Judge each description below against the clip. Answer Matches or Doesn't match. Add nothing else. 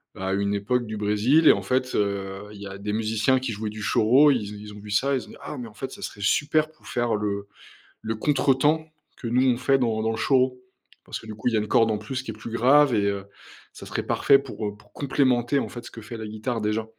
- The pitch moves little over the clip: Doesn't match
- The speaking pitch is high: Doesn't match